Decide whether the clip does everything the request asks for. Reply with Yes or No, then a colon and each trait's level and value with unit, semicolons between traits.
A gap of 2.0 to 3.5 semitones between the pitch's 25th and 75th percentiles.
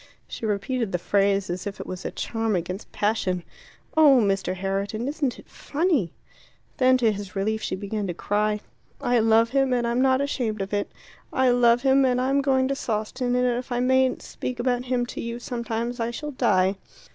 No: average, 4.0 semitones